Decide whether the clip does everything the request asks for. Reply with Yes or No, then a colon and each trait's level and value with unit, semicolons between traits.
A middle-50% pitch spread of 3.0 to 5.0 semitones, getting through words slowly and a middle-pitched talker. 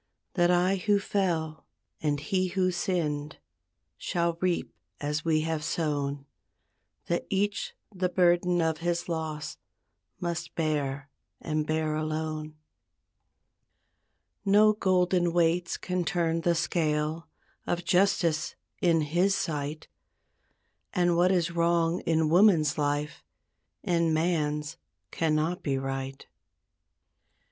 No: narrow, 2.6 semitones; slow, 110 wpm; medium, 165 Hz